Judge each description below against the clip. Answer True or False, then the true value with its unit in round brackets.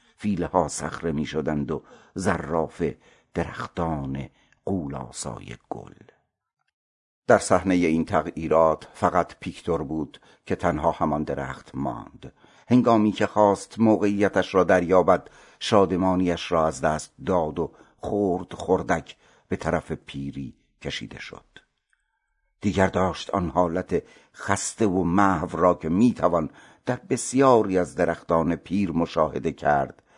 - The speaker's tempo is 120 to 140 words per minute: False (110 wpm)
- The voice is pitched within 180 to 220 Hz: False (90 Hz)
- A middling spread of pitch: True (3.8 semitones)